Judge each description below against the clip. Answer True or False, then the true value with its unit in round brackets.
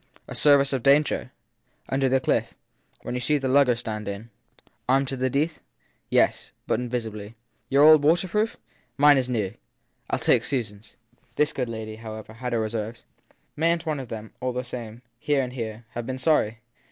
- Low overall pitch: True (125 Hz)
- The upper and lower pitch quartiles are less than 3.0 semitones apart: False (3.9 semitones)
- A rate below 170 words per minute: False (190 wpm)